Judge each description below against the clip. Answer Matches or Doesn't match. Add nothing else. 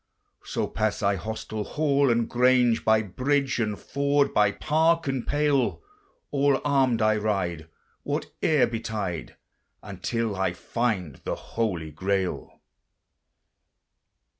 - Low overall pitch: Matches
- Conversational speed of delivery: Doesn't match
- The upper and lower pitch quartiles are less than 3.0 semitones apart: Doesn't match